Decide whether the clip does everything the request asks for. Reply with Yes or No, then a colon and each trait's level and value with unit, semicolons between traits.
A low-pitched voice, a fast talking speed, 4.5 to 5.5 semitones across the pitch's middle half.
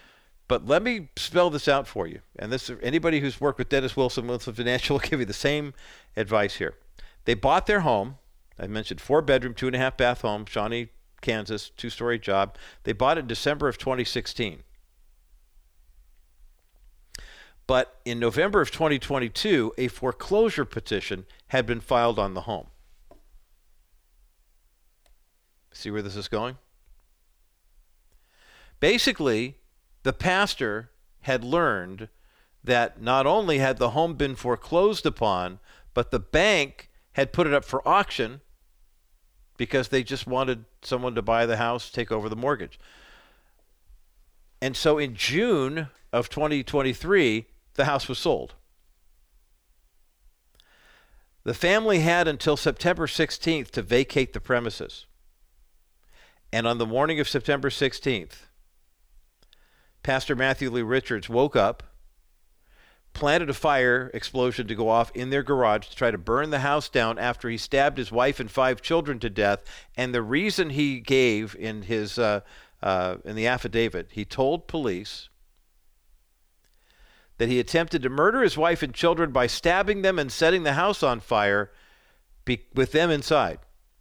No: low, 125 Hz; average, 145 wpm; average, 5.1 semitones